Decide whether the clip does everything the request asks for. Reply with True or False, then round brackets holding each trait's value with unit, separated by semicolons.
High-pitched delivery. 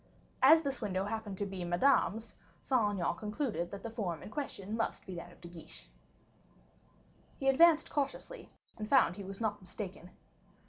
True (210 Hz)